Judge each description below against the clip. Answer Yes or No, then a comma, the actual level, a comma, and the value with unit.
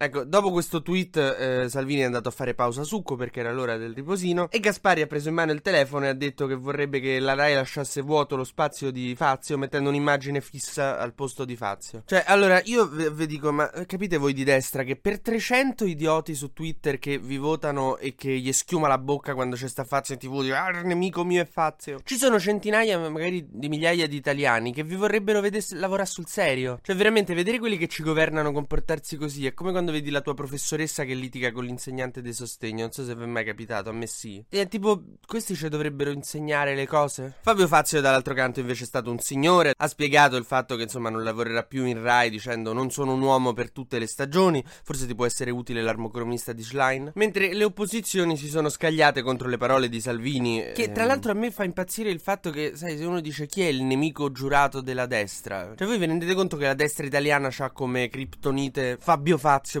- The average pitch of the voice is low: No, medium, 145 Hz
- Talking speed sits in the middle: No, fast, 225 wpm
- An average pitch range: Yes, average, 4.7 semitones